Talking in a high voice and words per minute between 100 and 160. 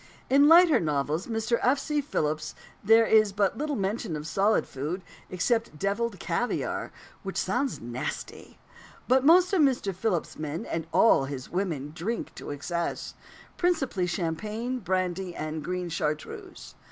Yes: high, 195 Hz; average, 150 wpm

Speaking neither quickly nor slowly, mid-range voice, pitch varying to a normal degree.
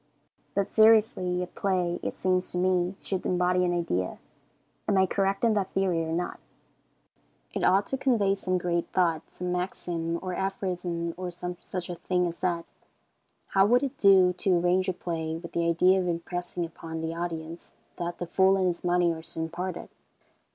No: average, 185 wpm; medium, 180 Hz; narrow, 1.8 semitones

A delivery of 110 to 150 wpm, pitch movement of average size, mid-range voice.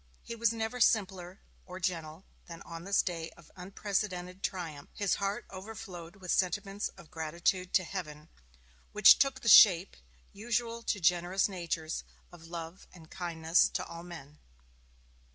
Yes: average, 145 wpm; average, 3.0 semitones; medium, 180 Hz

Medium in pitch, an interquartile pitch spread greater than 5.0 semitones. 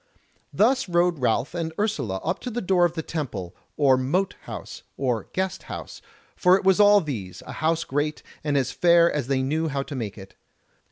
Yes: medium, 155 Hz; wide, 5.4 semitones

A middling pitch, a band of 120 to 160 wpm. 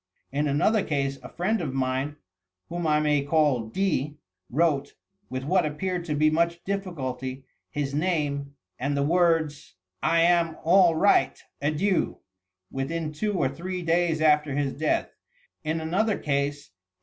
Yes: medium, 155 Hz; average, 150 wpm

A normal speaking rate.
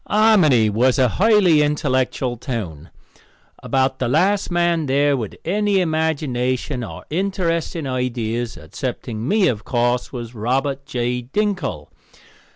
No: slow, 120 wpm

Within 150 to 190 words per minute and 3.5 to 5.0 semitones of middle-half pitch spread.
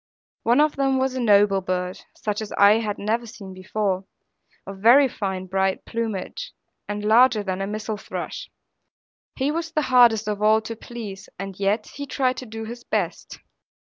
Yes: average, 180 wpm; average, 3.9 semitones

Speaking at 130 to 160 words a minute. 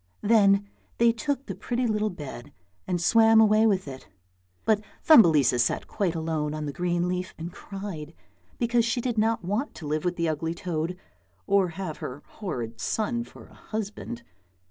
No: average, 170 wpm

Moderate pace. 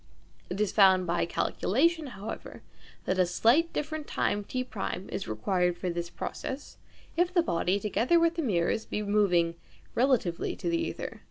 Yes: average, 160 wpm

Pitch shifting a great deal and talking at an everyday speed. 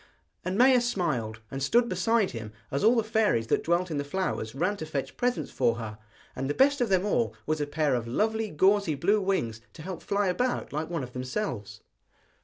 No: wide, 7.9 semitones; fast, 210 wpm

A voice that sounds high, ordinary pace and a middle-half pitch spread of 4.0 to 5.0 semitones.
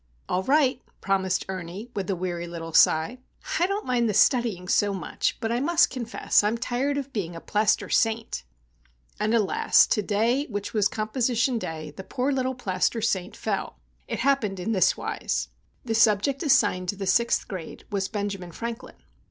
Yes: high, 215 Hz; average, 170 wpm; average, 4.5 semitones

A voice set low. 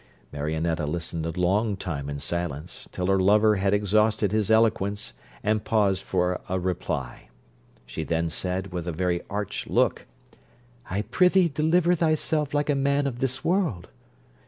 Yes: low, 100 Hz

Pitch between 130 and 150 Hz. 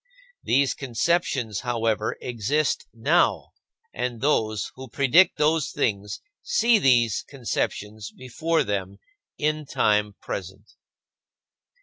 No: low, 120 Hz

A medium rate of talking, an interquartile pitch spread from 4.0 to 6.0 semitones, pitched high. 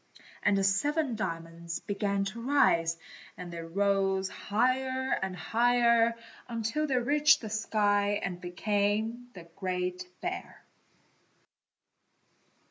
No: slow, 110 wpm; average, 4.6 semitones; high, 205 Hz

